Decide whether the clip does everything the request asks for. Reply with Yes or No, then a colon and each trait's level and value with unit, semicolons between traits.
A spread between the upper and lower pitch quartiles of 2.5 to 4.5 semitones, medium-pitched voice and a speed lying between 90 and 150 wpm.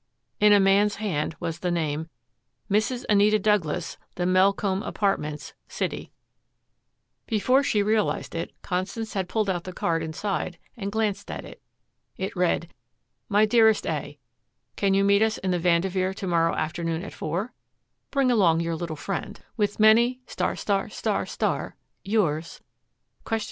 No: average, 3.7 semitones; high, 195 Hz; average, 140 wpm